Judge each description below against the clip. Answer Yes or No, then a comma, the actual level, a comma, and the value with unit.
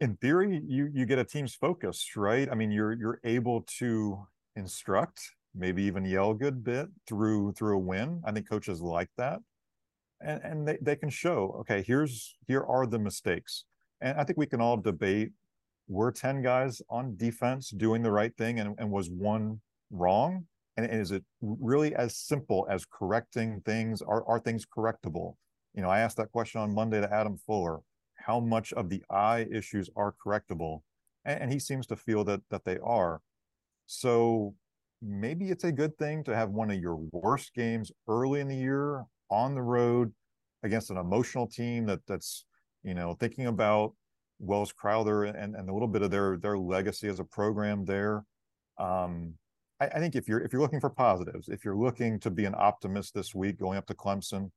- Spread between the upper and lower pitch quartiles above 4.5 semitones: No, average, 3.5 semitones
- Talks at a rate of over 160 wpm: Yes, average, 190 wpm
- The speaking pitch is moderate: No, low, 110 Hz